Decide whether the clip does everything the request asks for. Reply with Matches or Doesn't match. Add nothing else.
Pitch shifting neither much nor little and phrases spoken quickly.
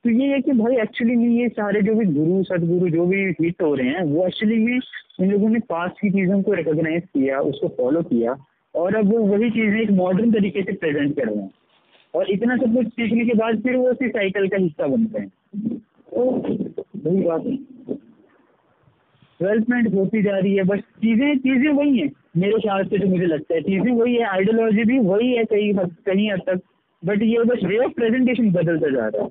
Matches